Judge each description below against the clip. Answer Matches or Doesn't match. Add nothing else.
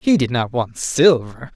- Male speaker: Matches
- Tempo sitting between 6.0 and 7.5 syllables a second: Doesn't match